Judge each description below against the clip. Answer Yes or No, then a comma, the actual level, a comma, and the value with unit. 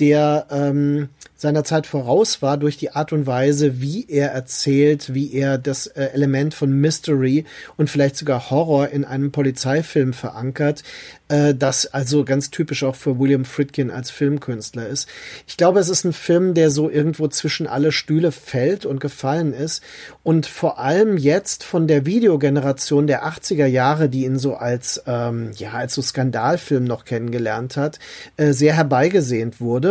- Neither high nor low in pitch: Yes, medium, 145 Hz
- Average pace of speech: Yes, average, 165 wpm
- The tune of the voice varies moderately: No, narrow, 2.3 semitones